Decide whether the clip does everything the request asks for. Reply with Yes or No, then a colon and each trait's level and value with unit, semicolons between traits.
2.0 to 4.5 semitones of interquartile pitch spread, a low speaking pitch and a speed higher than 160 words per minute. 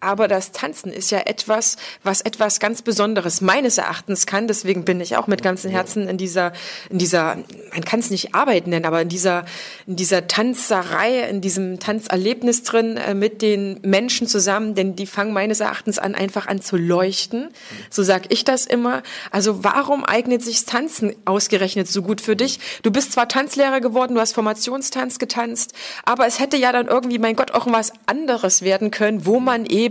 No: average, 3.6 semitones; high, 210 Hz; fast, 190 wpm